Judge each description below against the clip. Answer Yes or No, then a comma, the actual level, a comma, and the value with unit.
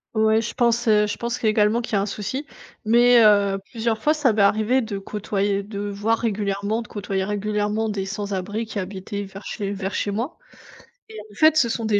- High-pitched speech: Yes, high, 210 Hz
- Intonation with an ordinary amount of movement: No, narrow, 2.1 semitones